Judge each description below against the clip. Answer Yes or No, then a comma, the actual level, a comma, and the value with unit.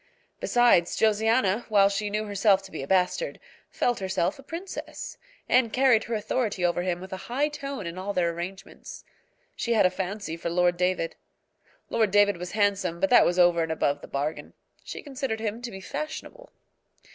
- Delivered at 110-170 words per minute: No, average, 185 wpm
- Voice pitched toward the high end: Yes, high, 200 Hz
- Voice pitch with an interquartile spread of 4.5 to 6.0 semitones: Yes, average, 4.8 semitones